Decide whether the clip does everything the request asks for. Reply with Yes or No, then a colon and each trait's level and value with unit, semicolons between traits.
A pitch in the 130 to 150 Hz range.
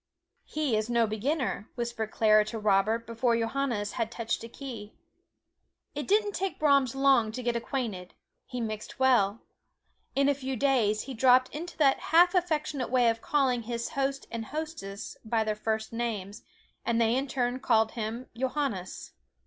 No: high, 240 Hz